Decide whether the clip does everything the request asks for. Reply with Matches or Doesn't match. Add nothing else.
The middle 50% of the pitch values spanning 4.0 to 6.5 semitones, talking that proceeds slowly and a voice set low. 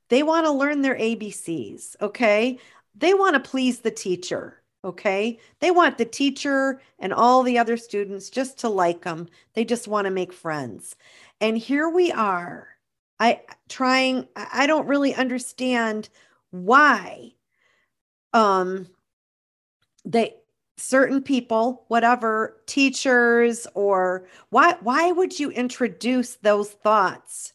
Doesn't match